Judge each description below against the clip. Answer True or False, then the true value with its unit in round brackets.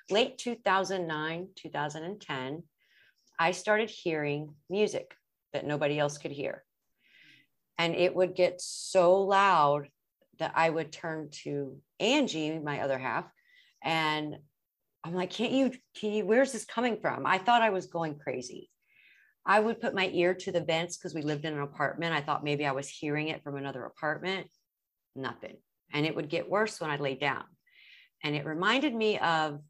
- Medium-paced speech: True (170 wpm)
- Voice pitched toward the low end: False (170 Hz)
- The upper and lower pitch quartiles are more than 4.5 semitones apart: True (4.9 semitones)